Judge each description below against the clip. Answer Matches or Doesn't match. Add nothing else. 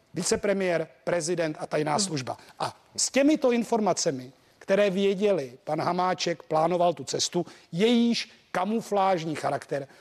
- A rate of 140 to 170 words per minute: Doesn't match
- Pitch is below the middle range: Doesn't match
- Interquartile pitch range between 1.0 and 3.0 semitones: Doesn't match